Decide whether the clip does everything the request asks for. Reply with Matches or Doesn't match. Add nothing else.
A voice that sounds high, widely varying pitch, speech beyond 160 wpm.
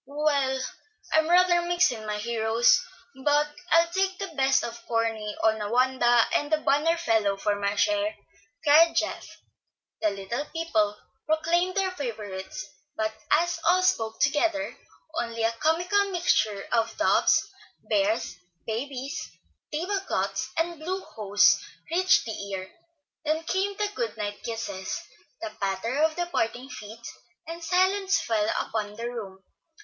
Doesn't match